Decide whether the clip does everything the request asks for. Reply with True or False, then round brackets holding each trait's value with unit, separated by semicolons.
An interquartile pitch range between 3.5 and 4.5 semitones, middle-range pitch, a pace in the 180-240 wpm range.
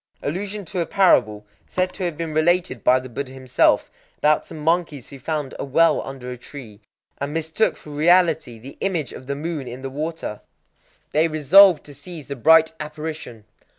True (3.9 semitones; 150 Hz; 185 wpm)